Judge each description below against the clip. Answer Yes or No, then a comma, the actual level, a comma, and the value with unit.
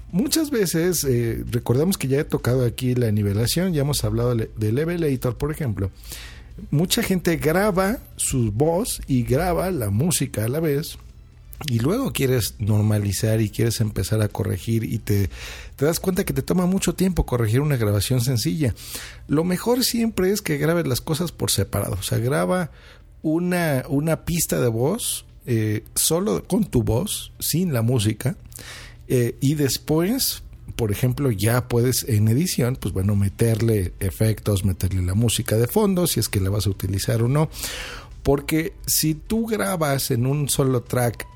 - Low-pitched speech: Yes, low, 130 Hz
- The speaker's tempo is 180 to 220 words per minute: No, average, 165 wpm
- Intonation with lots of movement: Yes, wide, 6.5 semitones